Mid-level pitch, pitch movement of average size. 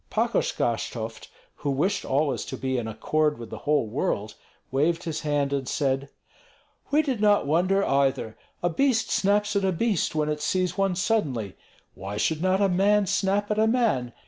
No: medium, 155 Hz; wide, 6.9 semitones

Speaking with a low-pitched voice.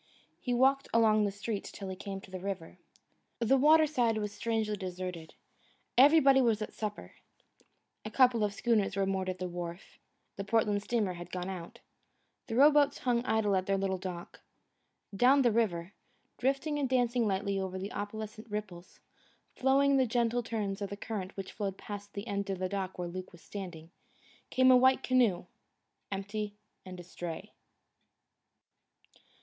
No: high, 205 Hz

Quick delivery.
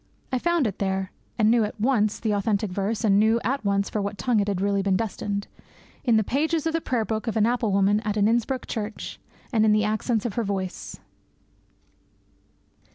Yes: fast, 210 wpm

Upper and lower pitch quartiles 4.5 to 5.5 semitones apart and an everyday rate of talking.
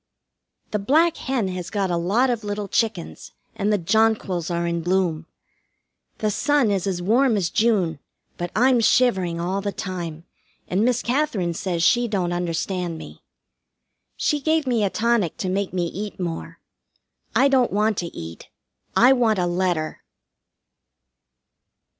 Yes: average, 4.8 semitones; average, 155 wpm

